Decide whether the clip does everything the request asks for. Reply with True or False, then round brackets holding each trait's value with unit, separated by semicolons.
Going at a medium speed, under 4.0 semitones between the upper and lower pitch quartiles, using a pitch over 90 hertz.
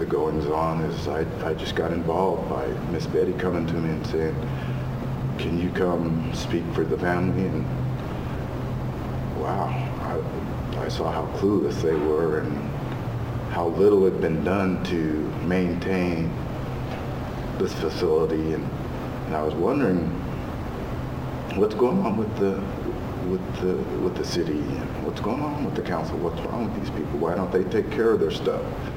False (160 wpm; 2.9 semitones; 85 Hz)